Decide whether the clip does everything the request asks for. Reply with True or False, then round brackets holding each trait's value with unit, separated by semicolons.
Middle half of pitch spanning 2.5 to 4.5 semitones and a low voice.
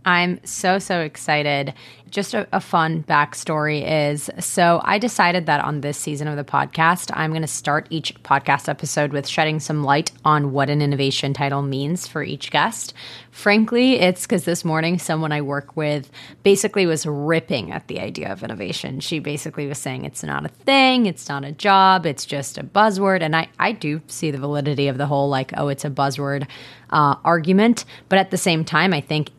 False (3.8 semitones; 155 Hz)